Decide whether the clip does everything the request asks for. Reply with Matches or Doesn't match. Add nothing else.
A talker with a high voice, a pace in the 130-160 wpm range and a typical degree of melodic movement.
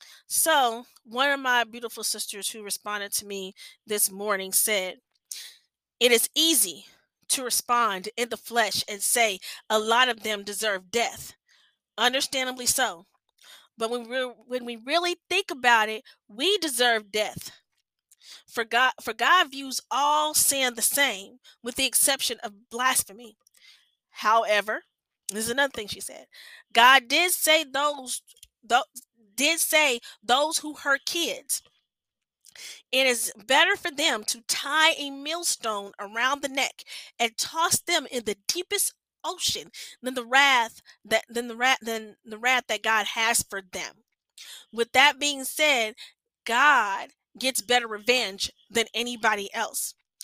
Matches